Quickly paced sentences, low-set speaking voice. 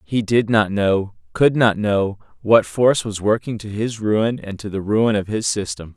Yes: fast, 210 wpm; low, 110 Hz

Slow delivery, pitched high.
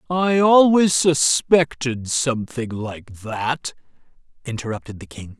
No: slow, 100 wpm; low, 135 Hz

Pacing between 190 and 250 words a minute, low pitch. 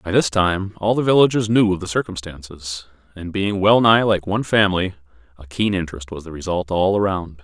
Yes: average, 195 wpm; very low, 95 Hz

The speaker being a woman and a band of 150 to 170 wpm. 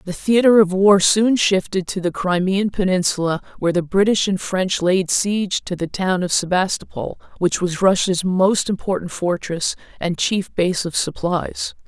Yes: female; average, 165 wpm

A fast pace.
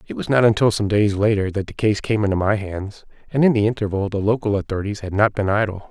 Yes: fast, 255 wpm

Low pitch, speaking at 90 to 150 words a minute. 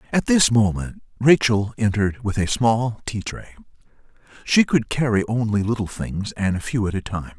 No: low, 110 Hz; average, 180 wpm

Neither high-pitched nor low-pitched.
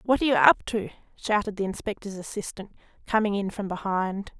No: high, 205 Hz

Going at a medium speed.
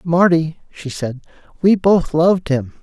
Yes: average, 150 wpm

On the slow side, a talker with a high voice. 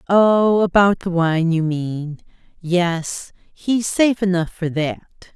No: slow, 125 wpm; medium, 180 Hz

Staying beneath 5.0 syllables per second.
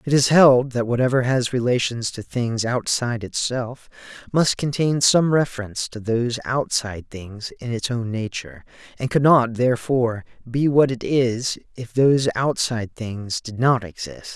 Yes: 4.7 syllables/s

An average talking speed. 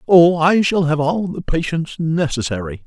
Yes: average, 170 wpm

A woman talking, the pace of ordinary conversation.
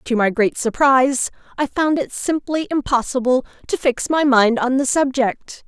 Yes: female; average, 170 wpm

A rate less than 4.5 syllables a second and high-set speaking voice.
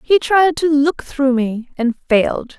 Yes: 4.0 syllables/s; very high, 280 Hz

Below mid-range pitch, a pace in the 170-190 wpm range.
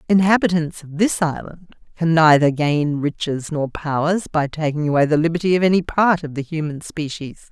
No: medium, 160 Hz; average, 175 wpm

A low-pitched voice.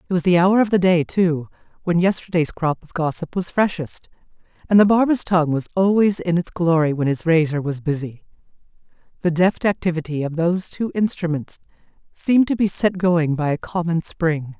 No: medium, 170 Hz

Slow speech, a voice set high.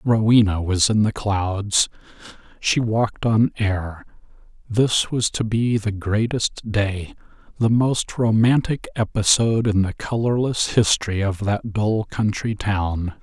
No: slow, 130 wpm; low, 105 Hz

